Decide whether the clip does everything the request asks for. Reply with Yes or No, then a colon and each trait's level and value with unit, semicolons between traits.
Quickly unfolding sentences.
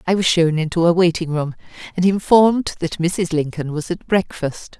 No: average, 190 wpm